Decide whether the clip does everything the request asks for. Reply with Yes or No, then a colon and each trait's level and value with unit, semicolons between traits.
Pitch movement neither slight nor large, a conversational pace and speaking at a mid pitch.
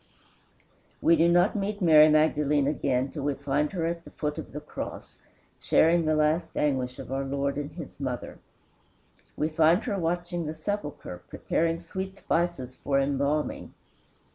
Yes: average, 3.2 semitones; average, 160 wpm; medium, 155 Hz